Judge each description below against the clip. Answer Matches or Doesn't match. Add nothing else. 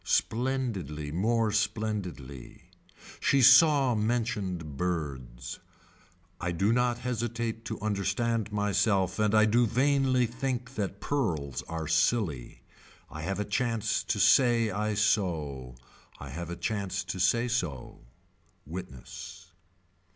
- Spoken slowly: Matches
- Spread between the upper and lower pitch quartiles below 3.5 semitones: Doesn't match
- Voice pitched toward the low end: Matches